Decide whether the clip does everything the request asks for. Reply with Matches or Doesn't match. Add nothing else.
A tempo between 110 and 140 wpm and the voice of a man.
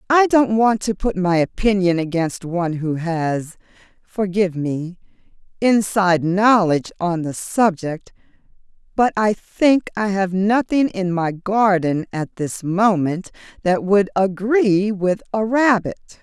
Doesn't match